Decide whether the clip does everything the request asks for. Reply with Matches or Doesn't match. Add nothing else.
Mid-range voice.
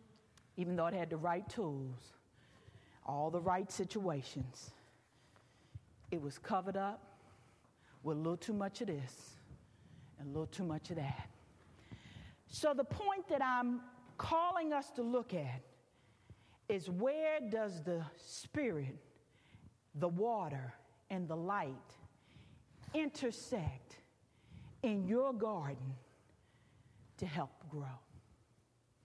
Matches